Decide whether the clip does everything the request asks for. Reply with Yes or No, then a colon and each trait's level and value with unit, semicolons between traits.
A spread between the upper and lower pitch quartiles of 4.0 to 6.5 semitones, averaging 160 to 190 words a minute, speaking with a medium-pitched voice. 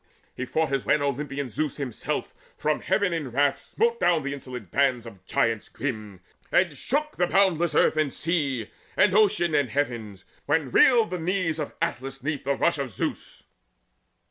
Yes: average, 4.9 semitones; average, 175 wpm; medium, 145 Hz